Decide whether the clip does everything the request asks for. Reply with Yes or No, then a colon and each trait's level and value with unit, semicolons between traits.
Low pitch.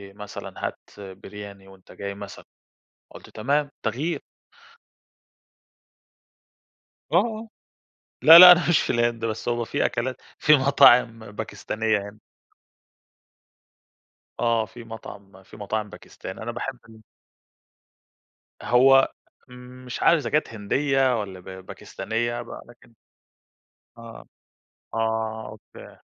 Yes: low, 115 Hz